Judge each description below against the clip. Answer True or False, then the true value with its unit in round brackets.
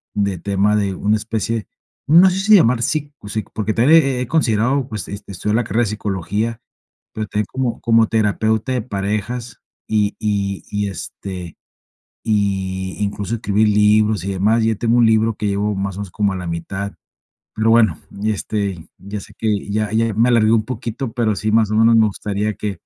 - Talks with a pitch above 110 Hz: False (105 Hz)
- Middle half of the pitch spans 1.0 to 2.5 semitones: True (2.2 semitones)